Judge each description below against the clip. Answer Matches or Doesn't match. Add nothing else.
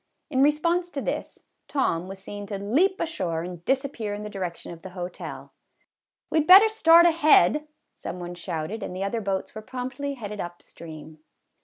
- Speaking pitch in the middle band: Doesn't match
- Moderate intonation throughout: Doesn't match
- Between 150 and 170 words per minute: Doesn't match